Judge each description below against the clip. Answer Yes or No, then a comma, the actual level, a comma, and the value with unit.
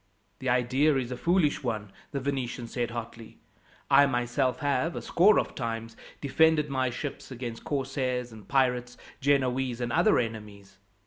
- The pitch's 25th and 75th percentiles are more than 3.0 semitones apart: No, average, 2.7 semitones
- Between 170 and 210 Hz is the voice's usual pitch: No, low, 125 Hz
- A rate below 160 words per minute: Yes, average, 150 wpm